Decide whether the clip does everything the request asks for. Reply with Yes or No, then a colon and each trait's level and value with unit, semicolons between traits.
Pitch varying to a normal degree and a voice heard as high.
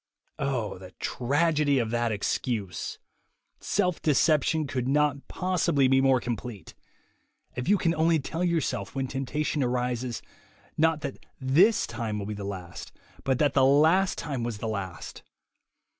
No: average, 4.5 semitones; low, 135 Hz